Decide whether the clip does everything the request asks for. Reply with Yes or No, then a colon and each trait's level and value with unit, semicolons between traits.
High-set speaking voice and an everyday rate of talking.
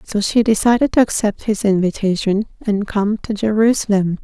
Yes: high, 210 Hz; average, 155 wpm